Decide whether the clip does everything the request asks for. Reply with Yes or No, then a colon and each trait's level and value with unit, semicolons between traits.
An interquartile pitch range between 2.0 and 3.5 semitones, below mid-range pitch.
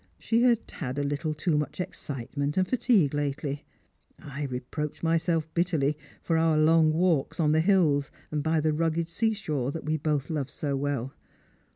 No: narrow, 2.6 semitones; medium, 155 Hz